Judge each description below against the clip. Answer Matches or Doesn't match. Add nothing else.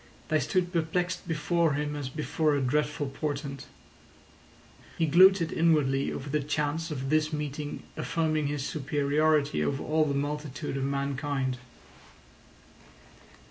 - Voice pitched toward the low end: Doesn't match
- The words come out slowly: Matches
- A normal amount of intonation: Doesn't match